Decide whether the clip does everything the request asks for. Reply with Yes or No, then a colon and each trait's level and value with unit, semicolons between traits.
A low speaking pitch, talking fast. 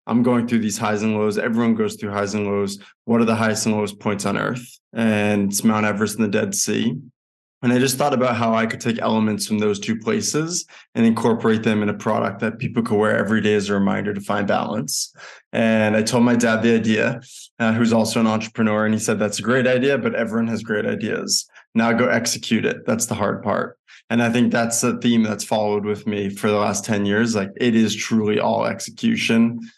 Yes: low, 115 Hz; fast, 230 wpm